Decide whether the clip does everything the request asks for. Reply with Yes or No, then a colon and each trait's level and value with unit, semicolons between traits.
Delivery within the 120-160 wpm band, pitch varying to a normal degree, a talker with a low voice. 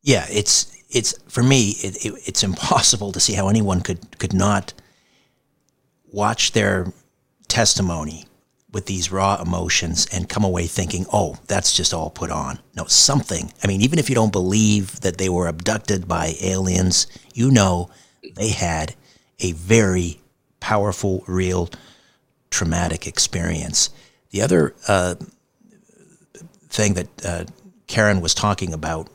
Yes: average, 140 wpm; average, 3.5 semitones; low, 100 Hz